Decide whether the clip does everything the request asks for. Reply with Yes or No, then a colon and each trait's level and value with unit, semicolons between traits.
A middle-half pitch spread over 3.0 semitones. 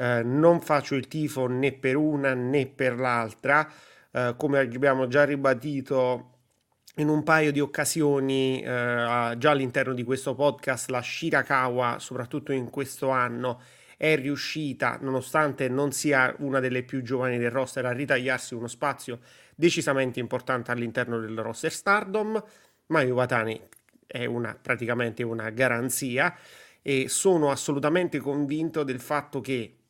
No: average, 2.7 semitones